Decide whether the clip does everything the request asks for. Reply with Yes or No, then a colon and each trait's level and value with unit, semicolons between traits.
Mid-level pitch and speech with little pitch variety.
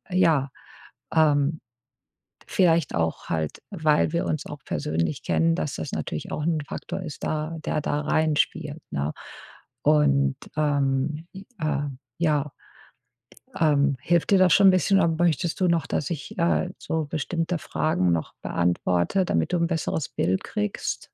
No: medium, 150 Hz; average, 3.5 semitones